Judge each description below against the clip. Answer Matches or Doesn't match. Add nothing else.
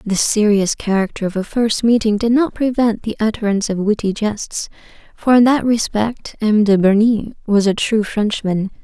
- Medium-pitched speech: Doesn't match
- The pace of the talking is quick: Doesn't match